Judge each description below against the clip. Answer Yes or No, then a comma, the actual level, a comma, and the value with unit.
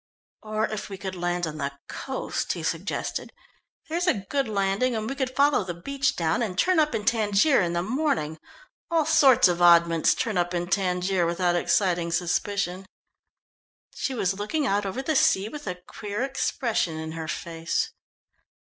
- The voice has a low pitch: No, high, 195 Hz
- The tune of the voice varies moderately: No, wide, 6.6 semitones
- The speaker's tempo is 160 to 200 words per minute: Yes, average, 170 wpm